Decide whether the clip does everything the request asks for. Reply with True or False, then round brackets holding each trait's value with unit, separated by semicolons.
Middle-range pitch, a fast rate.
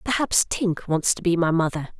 True (180 Hz; 210 wpm)